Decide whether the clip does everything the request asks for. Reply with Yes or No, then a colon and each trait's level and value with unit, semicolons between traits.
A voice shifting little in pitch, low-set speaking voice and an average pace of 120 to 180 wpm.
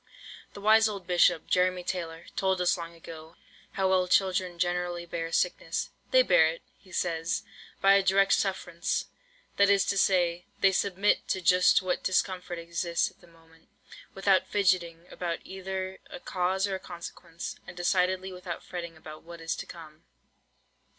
No: narrow, 2.0 semitones; medium, 180 Hz; average, 165 wpm